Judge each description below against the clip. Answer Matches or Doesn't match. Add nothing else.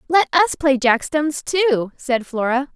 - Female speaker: Matches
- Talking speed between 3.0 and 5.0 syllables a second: Matches